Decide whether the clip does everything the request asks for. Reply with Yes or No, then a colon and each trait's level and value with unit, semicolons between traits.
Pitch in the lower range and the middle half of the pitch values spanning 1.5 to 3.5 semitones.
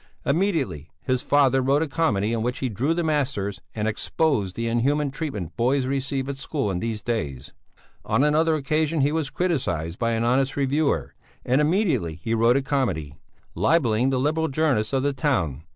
No: low, 130 Hz; average, 5.0 semitones